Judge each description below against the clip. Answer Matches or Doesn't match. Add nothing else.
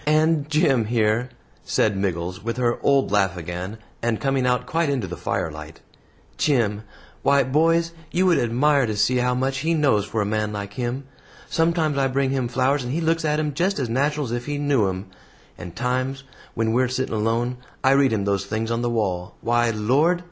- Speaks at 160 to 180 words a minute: Doesn't match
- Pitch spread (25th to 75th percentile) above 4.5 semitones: Matches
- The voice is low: Matches